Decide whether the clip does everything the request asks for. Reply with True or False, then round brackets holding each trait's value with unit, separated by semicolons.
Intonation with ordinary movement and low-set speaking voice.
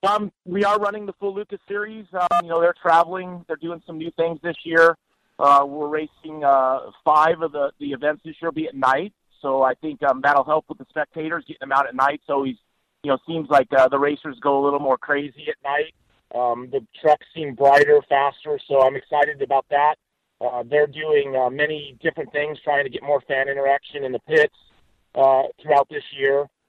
False (3.1 semitones; 150 Hz)